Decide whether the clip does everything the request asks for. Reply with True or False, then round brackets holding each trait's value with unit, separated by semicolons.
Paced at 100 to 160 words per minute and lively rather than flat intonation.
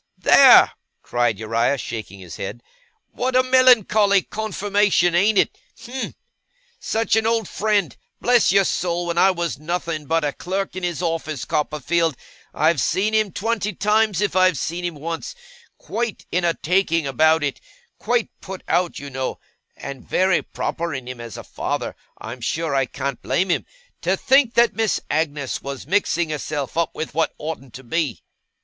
False (170 wpm; 6.0 semitones)